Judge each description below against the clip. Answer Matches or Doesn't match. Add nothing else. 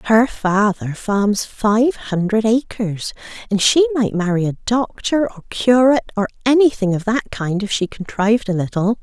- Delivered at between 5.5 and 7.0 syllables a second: Doesn't match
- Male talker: Doesn't match